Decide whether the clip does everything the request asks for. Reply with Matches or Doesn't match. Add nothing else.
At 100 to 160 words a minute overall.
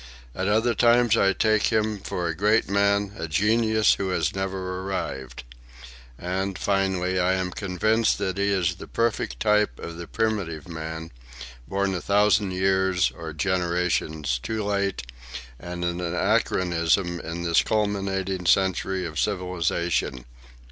Matches